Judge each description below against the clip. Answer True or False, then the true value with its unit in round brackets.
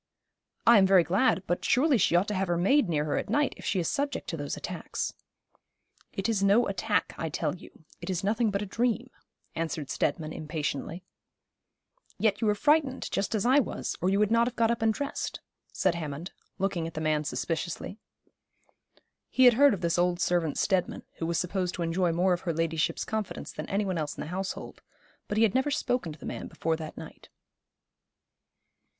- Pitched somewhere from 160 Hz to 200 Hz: True (190 Hz)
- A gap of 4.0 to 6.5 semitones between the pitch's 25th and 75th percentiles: True (5.3 semitones)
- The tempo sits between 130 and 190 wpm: False (205 wpm)